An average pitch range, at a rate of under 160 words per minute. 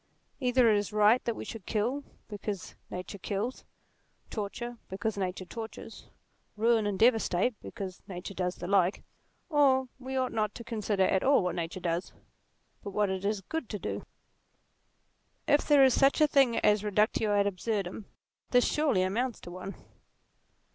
No: average, 4.2 semitones; average, 165 wpm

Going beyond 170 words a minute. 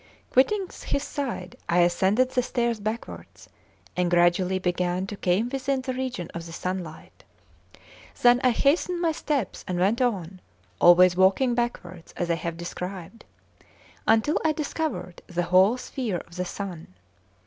No: average, 150 wpm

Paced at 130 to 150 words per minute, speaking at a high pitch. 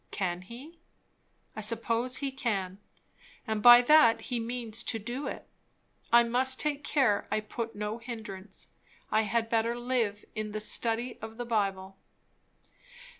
Yes: average, 140 wpm; high, 230 Hz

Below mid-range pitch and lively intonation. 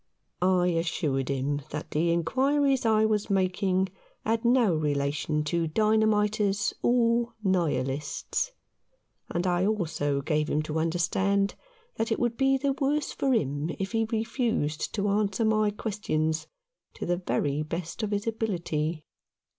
No: high, 190 Hz; wide, 6.0 semitones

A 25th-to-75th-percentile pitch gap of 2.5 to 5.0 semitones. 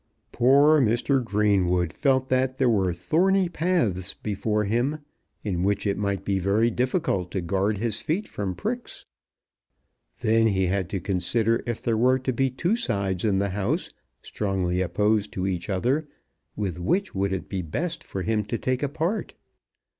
No: wide, 5.4 semitones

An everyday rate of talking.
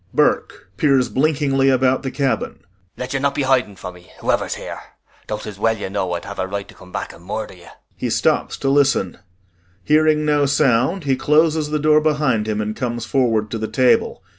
No: fast, 215 wpm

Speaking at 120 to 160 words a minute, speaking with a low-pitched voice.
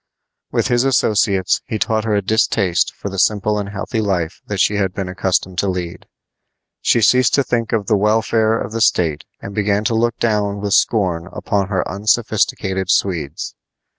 No: average, 180 wpm; low, 100 Hz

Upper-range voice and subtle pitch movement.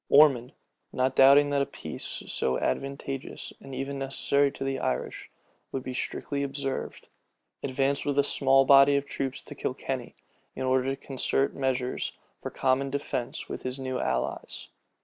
No: low, 135 Hz; narrow, 1.1 semitones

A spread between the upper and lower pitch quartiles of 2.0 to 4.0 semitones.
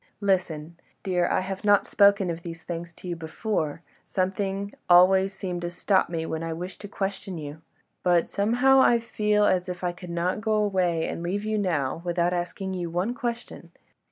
Yes: average, 2.8 semitones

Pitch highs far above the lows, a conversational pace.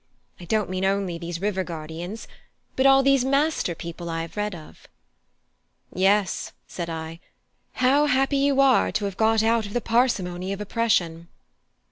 Yes: wide, 6.1 semitones; average, 160 wpm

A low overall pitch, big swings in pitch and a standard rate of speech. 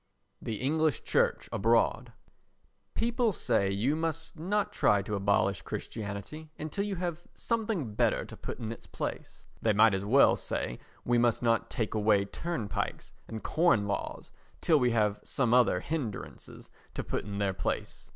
Yes: low, 115 Hz; wide, 7.5 semitones; average, 160 wpm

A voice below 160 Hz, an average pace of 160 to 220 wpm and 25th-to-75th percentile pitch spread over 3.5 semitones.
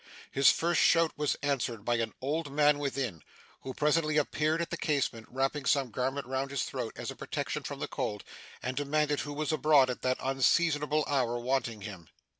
No: medium, 140 Hz; average, 190 wpm; average, 3.0 semitones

